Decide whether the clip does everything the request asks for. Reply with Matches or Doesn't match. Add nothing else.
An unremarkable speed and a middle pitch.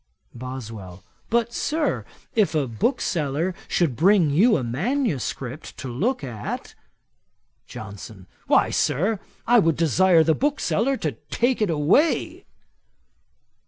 Doesn't match